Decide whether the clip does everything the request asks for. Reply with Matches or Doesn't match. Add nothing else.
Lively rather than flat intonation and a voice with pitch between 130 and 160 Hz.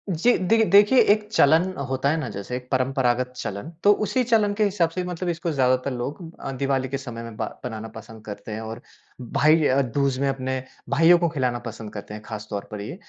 Matches